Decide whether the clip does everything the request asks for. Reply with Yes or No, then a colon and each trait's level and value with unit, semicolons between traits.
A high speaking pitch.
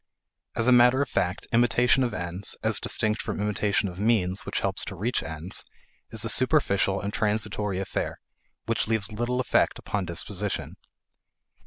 No: low, 105 Hz